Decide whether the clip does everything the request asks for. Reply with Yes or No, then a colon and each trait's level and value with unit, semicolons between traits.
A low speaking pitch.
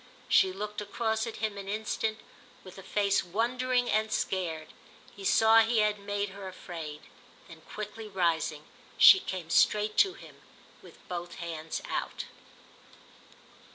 No: high, 205 Hz